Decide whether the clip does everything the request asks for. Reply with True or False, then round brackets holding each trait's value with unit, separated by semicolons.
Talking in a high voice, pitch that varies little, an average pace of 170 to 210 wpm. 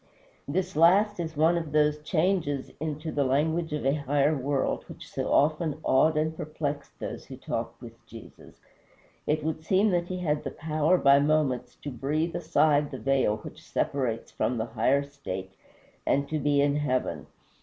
False (150 Hz; 2.2 semitones; 175 wpm)